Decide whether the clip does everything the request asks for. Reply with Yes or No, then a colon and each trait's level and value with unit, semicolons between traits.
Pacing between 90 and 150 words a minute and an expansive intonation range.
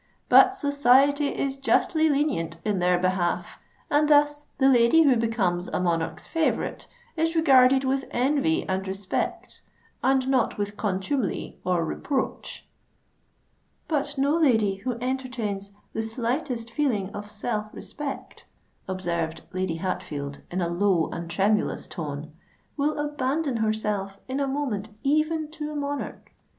Yes: slow, 135 wpm; wide, 6.9 semitones